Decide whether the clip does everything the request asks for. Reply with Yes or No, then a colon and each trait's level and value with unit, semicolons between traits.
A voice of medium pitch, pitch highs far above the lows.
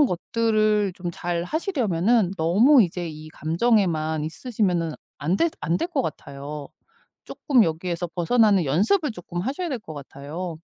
Yes: medium, 180 Hz; wide, 6.0 semitones